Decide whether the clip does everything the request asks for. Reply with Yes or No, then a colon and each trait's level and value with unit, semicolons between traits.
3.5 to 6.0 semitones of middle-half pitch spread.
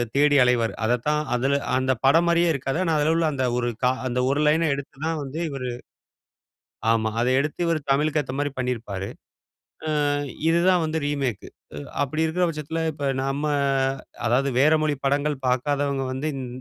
No: average, 3.1 semitones